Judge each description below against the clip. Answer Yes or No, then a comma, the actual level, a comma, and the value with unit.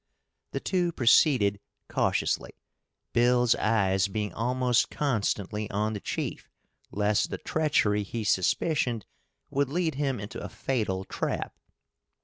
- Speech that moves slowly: Yes, slow, 120 wpm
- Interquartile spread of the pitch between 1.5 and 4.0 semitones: No, average, 4.4 semitones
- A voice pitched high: No, low, 115 Hz